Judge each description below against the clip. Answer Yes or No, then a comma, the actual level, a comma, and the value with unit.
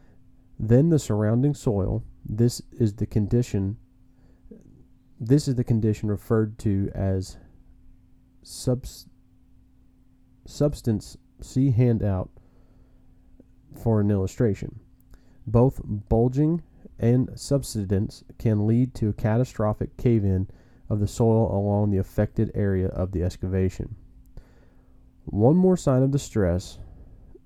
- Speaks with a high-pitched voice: No, low, 115 Hz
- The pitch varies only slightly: No, average, 4.1 semitones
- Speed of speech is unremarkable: No, slow, 105 wpm